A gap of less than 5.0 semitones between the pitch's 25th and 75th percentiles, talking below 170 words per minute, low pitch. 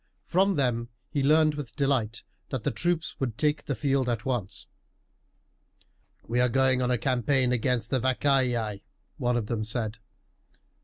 Yes: average, 3.0 semitones; average, 155 wpm; low, 125 Hz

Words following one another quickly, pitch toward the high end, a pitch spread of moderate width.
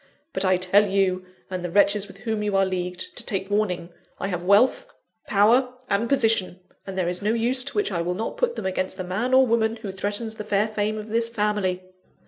Yes: fast, 225 wpm; high, 205 Hz; average, 3.2 semitones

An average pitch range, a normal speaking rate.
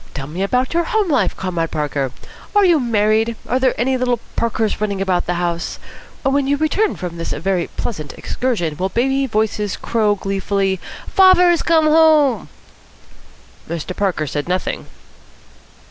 No: wide, 7.0 semitones; average, 150 wpm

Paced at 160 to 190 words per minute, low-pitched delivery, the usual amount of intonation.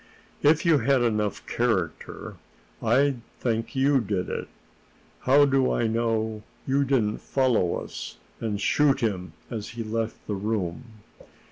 No: slow, 135 wpm; low, 115 Hz; average, 4.0 semitones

